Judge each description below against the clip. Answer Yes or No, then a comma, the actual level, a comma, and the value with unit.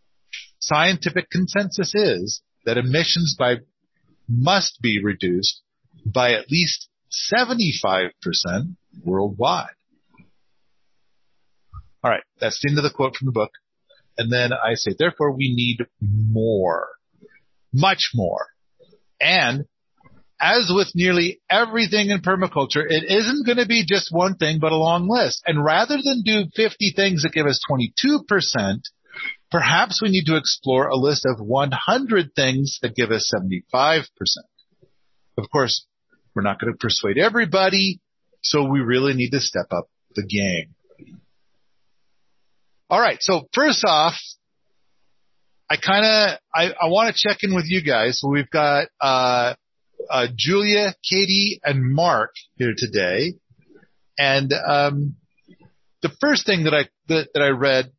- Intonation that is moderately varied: No, wide, 7.3 semitones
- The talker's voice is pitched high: No, medium, 150 Hz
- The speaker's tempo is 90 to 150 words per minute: Yes, average, 140 wpm